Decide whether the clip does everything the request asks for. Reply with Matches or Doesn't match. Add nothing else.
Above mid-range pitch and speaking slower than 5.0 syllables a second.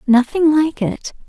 Matches